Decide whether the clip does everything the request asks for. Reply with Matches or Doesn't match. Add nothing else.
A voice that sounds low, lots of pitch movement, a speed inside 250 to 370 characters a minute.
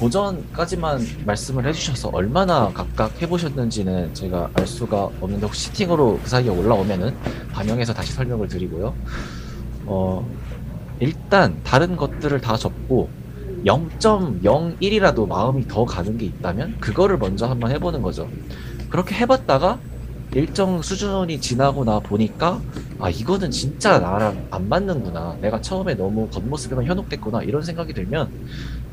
Matches